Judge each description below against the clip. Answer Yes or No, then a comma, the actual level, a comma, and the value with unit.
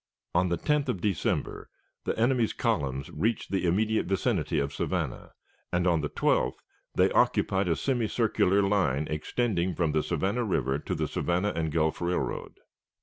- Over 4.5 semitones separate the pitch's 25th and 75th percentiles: Yes, average, 5.3 semitones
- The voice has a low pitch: Yes, very low, 90 Hz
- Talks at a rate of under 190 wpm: Yes, average, 155 wpm